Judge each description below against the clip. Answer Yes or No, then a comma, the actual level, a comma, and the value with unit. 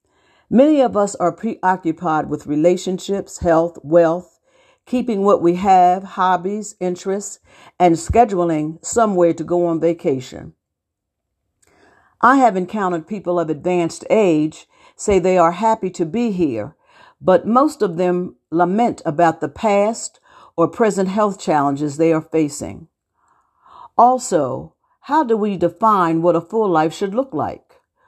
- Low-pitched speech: No, medium, 180 Hz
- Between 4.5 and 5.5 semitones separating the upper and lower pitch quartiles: Yes, average, 4.8 semitones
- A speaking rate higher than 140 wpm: No, slow, 135 wpm